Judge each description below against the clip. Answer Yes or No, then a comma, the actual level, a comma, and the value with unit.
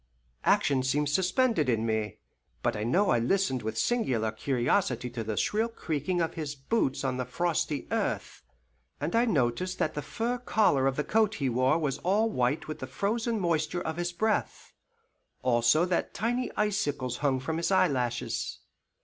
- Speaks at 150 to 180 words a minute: Yes, average, 170 wpm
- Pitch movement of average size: No, wide, 7.3 semitones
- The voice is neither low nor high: Yes, medium, 150 Hz